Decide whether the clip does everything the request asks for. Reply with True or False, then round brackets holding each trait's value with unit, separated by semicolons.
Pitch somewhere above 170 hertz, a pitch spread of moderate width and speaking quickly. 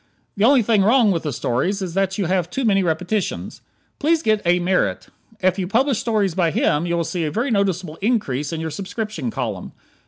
True (190 Hz; 4.3 semitones; 210 wpm)